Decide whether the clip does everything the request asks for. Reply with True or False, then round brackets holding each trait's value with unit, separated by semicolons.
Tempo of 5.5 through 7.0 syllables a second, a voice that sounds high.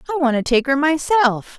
True (5.8 syllables/s; 285 Hz)